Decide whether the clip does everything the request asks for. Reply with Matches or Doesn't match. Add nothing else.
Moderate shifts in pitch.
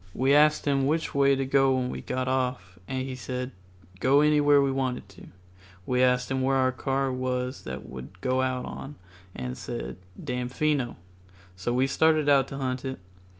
Doesn't match